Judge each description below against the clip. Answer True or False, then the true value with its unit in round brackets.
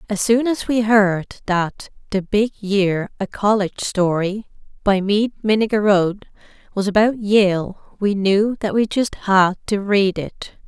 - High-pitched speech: True (205 Hz)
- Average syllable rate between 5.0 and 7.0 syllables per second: False (4.2 syllables/s)